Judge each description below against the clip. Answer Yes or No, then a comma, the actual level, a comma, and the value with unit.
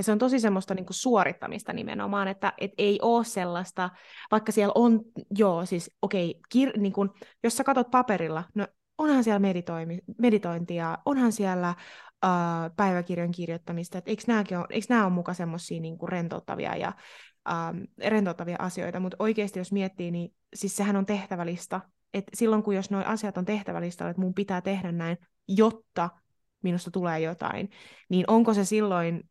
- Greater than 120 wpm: Yes, fast, 155 wpm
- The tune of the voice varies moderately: Yes, average, 3.4 semitones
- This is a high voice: Yes, high, 195 Hz